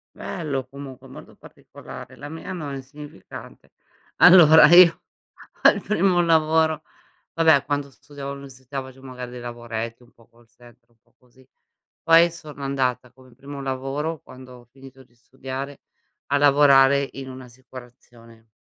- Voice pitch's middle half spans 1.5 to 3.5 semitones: Yes, average, 2.7 semitones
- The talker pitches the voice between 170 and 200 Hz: No, low, 135 Hz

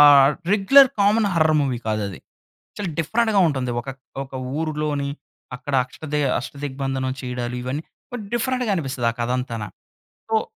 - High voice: No, medium, 145 Hz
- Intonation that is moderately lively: No, wide, 6.0 semitones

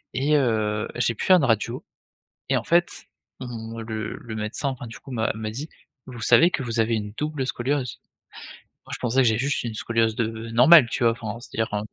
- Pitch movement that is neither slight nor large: Yes, average, 3.1 semitones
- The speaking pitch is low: Yes, low, 115 Hz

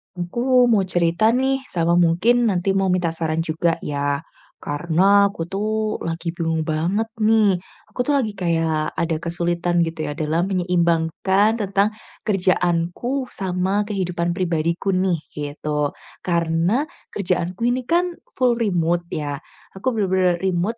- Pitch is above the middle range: No, medium, 180 Hz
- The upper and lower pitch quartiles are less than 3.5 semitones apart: No, average, 3.8 semitones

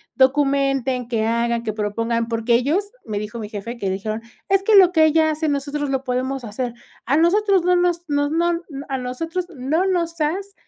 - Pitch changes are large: Yes, wide, 6.2 semitones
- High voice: Yes, very high, 275 Hz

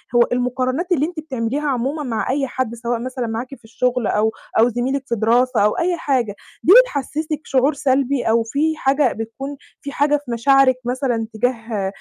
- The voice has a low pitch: No, very high, 255 Hz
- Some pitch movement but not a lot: Yes, average, 3.3 semitones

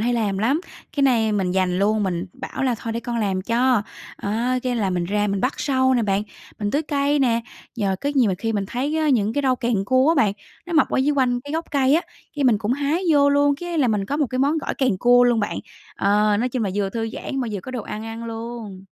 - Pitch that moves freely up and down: No, average, 4.7 semitones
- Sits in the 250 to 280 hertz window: No, high, 235 Hz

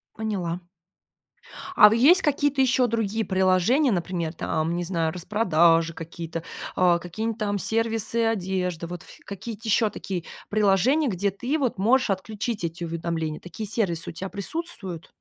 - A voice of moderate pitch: No, high, 195 Hz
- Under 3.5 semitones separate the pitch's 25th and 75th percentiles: No, average, 4.8 semitones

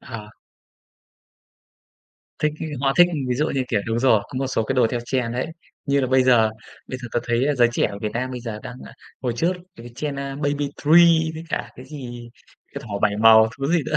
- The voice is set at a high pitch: No, low, 130 Hz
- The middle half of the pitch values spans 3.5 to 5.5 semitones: No, average, 3.1 semitones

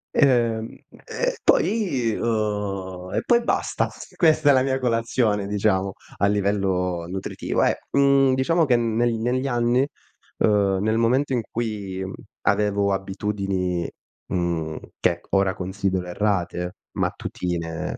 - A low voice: Yes, low, 105 Hz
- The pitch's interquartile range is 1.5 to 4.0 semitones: No, average, 4.6 semitones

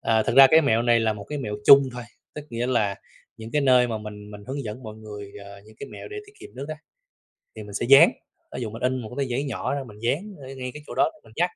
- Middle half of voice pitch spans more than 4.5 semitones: No, average, 4.2 semitones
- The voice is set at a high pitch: No, low, 120 Hz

